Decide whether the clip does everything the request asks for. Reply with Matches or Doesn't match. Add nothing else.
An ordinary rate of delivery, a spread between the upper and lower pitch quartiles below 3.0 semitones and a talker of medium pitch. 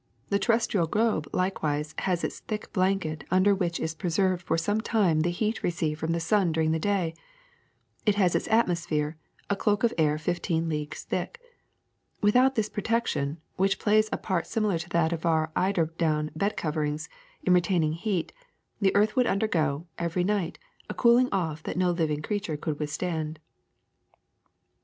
Doesn't match